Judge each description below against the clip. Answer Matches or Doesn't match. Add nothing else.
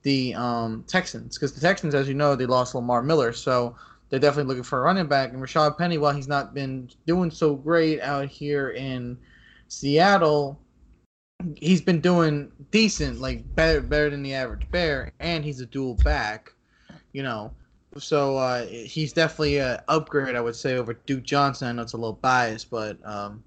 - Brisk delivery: Doesn't match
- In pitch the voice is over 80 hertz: Matches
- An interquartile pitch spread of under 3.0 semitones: Doesn't match